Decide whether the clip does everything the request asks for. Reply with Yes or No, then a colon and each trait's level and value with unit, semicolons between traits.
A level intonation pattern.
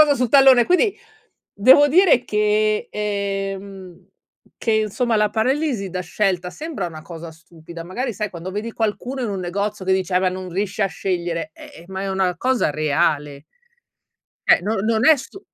No: average, 4.3 semitones